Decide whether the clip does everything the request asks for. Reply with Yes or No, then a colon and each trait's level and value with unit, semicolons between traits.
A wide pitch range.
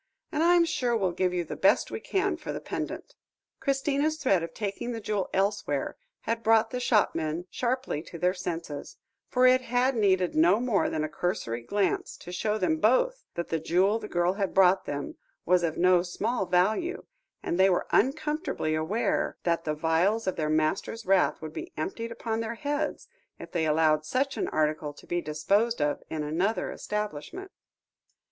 Yes: wide, 6.4 semitones